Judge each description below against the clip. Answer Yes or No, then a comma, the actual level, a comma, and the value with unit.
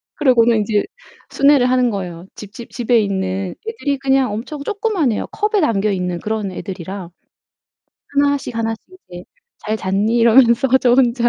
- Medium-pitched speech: No, high, 230 Hz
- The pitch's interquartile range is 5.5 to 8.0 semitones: No, average, 5.1 semitones